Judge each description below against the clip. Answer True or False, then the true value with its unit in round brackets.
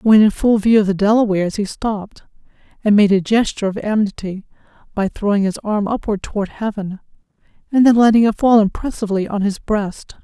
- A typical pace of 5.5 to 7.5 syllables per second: True (5.7 syllables/s)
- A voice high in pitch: True (210 Hz)